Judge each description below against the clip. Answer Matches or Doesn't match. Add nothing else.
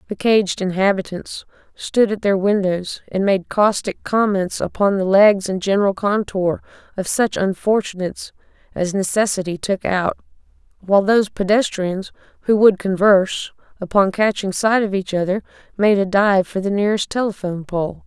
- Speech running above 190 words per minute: Doesn't match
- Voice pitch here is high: Matches